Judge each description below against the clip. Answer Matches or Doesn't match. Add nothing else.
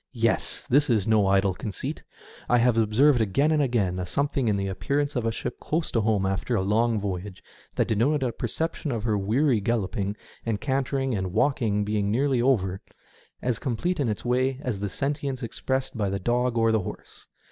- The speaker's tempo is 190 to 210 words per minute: Matches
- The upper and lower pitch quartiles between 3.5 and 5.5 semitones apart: Matches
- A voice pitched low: Matches